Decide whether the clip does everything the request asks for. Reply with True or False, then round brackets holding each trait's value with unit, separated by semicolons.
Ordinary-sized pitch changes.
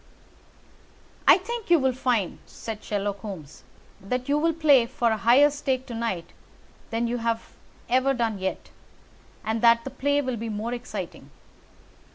True (3.5 semitones)